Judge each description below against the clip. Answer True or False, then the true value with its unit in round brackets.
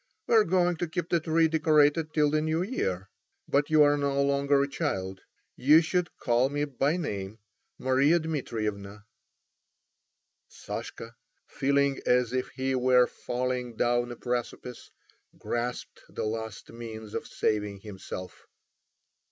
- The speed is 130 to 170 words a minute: True (135 wpm)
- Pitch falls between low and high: False (130 Hz)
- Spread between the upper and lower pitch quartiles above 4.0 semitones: True (5.2 semitones)